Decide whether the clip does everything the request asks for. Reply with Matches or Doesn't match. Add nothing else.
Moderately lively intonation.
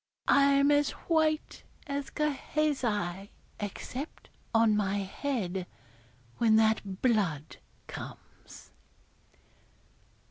Doesn't match